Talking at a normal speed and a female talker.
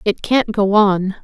Yes: average, 195 wpm; female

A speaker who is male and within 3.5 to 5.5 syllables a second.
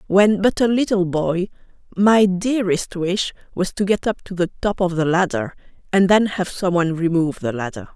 No: female; 5.1 syllables/s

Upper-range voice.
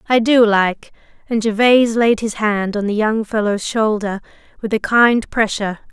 Yes: high, 215 Hz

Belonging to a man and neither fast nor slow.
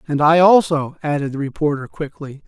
Yes: male; average, 170 wpm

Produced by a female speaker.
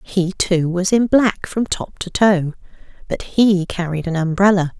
Yes: female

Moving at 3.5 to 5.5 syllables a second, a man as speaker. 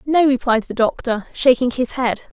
No: 4.6 syllables/s; female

